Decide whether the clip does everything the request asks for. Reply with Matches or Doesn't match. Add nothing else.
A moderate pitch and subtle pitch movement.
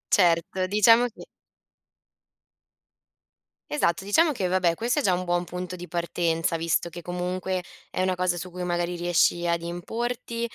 Matches